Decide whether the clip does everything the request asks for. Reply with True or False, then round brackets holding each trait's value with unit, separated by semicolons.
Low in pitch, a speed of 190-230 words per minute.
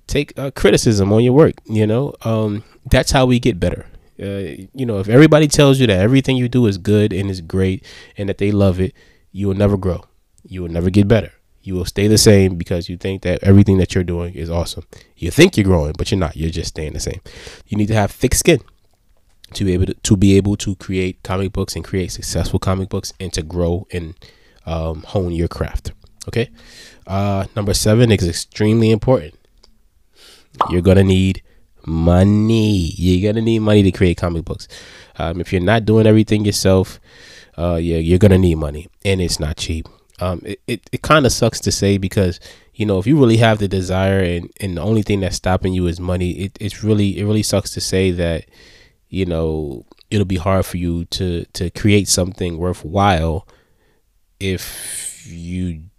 True (95 Hz; 205 wpm)